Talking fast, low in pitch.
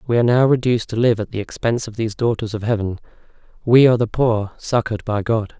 Yes: fast, 225 wpm; low, 115 Hz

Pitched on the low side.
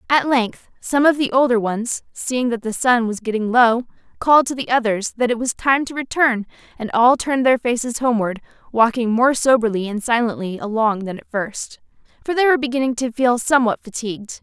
No: high, 240 Hz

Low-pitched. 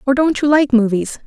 No: very high, 265 Hz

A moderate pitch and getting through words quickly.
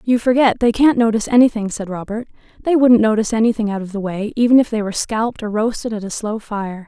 No: high, 220 Hz; fast, 235 wpm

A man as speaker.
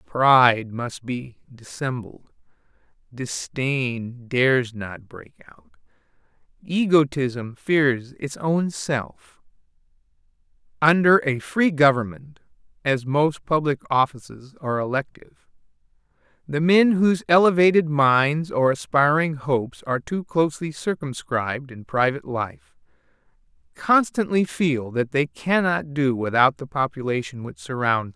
Yes: male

